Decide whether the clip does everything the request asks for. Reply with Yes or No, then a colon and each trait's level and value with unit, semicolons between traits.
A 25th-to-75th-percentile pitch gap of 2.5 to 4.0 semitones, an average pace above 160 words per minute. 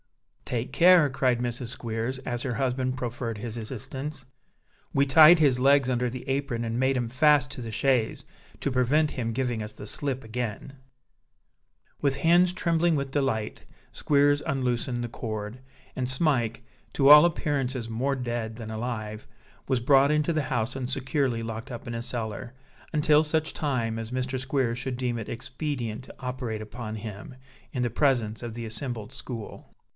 Yes: average, 3.1 semitones; average, 170 wpm